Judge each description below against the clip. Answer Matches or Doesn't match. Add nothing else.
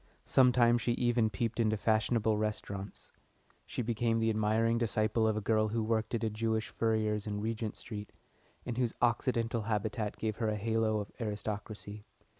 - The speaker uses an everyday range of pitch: Doesn't match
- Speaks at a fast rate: Doesn't match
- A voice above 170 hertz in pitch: Doesn't match